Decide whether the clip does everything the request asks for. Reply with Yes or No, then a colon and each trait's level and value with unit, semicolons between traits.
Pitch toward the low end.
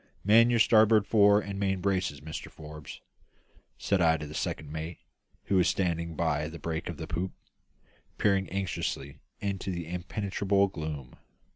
Yes: very low, 90 Hz